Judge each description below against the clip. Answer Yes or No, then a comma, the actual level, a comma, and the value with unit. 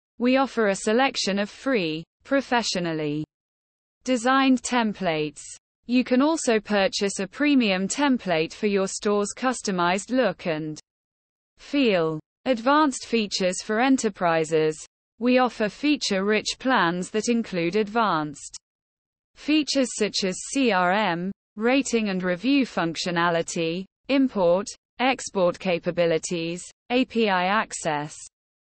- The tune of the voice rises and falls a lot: Yes, wide, 6.4 semitones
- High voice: Yes, high, 205 Hz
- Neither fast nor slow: No, slow, 100 wpm